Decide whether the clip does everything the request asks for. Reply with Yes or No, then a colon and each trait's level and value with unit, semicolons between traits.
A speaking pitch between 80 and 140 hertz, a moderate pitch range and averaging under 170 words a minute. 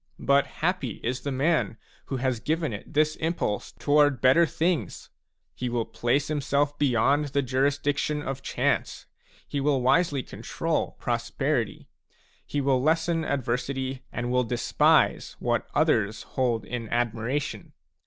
Yes: low, 135 Hz; average, 3.0 semitones; slow, 135 wpm